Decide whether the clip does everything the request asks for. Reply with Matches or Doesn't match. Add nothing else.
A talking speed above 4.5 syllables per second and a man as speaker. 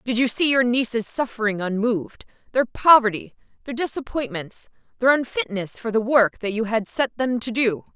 Doesn't match